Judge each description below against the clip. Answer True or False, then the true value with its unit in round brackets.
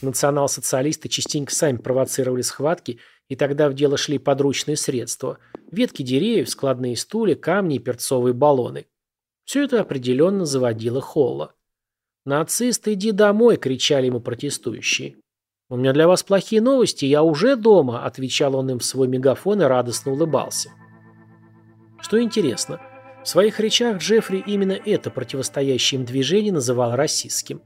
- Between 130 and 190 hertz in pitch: True (140 Hz)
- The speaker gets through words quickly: False (135 wpm)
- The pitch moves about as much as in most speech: False (7.1 semitones)